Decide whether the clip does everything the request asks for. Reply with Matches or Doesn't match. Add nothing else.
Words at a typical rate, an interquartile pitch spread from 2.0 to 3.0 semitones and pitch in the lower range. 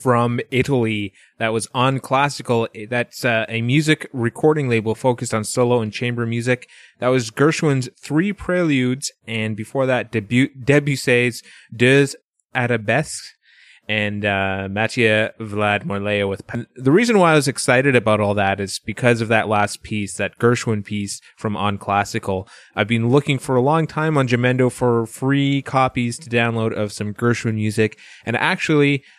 Doesn't match